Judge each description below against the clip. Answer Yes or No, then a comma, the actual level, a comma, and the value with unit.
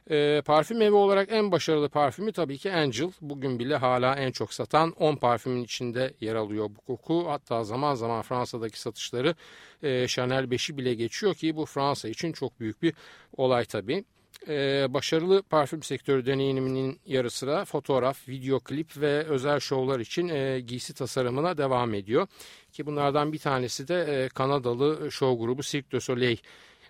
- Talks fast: Yes, fast, 160 wpm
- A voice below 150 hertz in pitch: Yes, low, 135 Hz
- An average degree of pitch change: Yes, average, 3.2 semitones